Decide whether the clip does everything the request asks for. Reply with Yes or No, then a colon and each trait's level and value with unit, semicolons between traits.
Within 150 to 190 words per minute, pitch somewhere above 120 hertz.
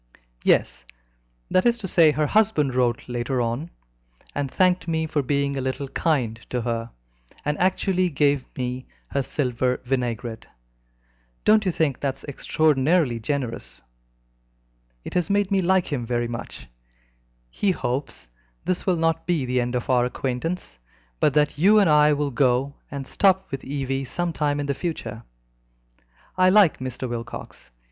Yes: average, 160 wpm; medium, 140 Hz